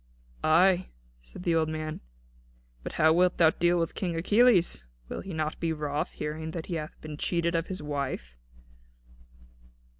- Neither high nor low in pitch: Yes, medium, 160 Hz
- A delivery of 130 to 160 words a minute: No, average, 170 wpm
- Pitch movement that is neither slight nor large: No, narrow, 2.2 semitones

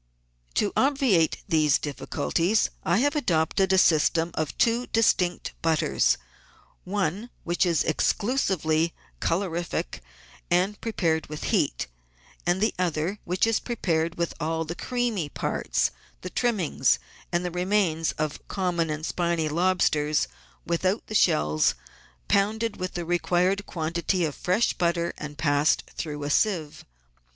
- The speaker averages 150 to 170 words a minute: No, slow, 135 wpm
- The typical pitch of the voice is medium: Yes, medium, 175 Hz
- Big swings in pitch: No, average, 3.7 semitones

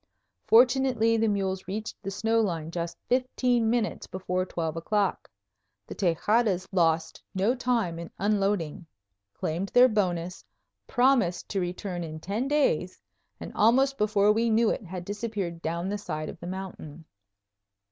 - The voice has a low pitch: No, high, 195 Hz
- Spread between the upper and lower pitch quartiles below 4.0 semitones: No, average, 4.6 semitones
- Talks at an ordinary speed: Yes, average, 145 wpm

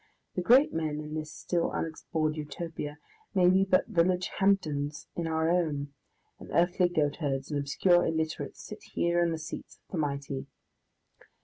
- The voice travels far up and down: No, average, 2.9 semitones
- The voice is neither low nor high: Yes, medium, 160 Hz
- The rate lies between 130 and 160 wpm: Yes, average, 155 wpm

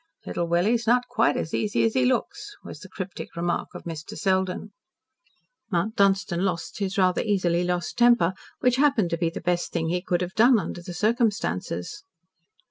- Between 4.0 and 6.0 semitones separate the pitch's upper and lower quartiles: Yes, average, 4.8 semitones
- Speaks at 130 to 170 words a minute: No, average, 180 wpm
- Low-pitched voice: No, high, 190 Hz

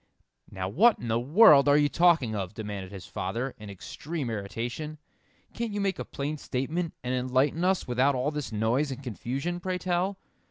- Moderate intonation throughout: No, wide, 6.6 semitones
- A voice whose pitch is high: No, low, 135 Hz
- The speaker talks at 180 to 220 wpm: Yes, average, 185 wpm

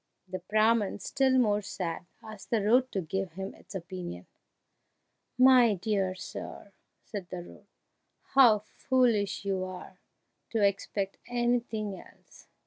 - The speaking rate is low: Yes, slow, 130 wpm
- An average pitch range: Yes, average, 3.6 semitones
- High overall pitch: Yes, high, 205 Hz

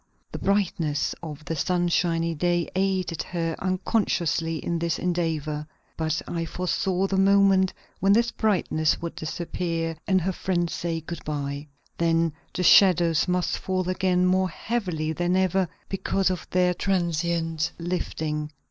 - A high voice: No, medium, 175 Hz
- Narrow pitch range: Yes, narrow, 2.3 semitones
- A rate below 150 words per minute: Yes, average, 140 wpm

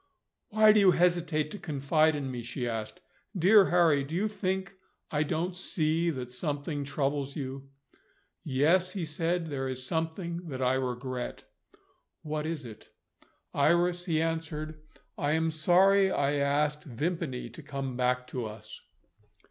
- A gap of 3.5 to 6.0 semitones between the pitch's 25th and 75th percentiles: Yes, average, 4.3 semitones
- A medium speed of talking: Yes, average, 150 wpm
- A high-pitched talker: No, medium, 155 Hz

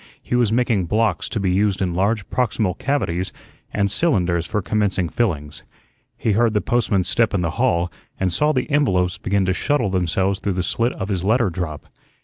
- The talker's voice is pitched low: Yes, low, 100 Hz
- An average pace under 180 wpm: No, average, 190 wpm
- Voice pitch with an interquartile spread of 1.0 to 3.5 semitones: No, average, 4.1 semitones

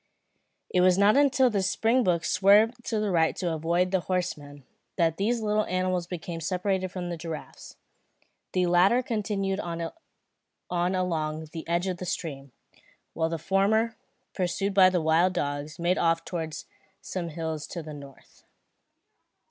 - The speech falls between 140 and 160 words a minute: Yes, average, 150 wpm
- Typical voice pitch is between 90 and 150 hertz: No, medium, 180 Hz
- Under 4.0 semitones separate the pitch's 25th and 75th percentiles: Yes, average, 3.0 semitones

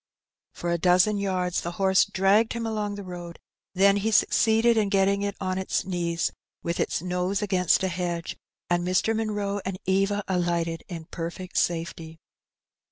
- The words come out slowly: No, average, 165 wpm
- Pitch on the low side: No, medium, 185 Hz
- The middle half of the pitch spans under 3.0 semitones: Yes, narrow, 2.5 semitones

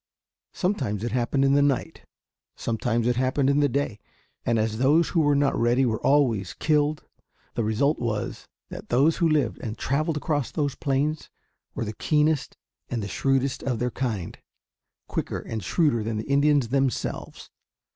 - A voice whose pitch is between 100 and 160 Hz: Yes, low, 135 Hz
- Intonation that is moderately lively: Yes, average, 4.0 semitones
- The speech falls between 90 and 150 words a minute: No, average, 165 wpm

